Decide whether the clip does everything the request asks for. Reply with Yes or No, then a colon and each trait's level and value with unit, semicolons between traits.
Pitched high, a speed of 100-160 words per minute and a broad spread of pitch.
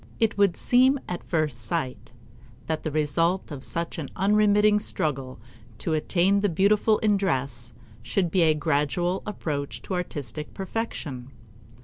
No: medium, 170 Hz; average, 140 wpm; wide, 5.8 semitones